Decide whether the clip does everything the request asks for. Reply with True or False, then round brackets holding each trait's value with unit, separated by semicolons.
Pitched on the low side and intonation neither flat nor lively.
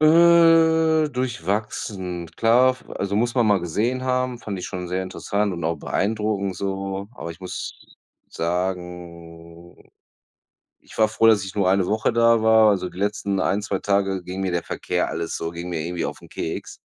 True (100 Hz; 4.0 semitones)